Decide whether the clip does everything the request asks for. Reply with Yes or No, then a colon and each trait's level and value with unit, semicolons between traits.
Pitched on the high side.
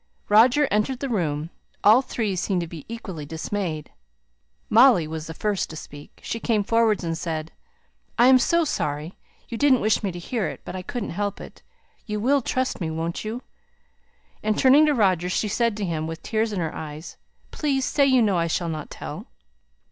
Yes: high, 205 Hz